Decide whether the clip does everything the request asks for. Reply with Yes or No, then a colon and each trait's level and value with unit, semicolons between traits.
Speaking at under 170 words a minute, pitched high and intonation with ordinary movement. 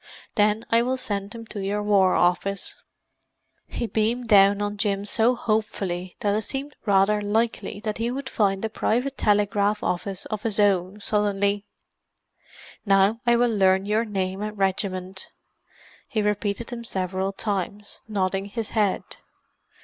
No: average, 150 wpm; high, 205 Hz; narrow, 2.1 semitones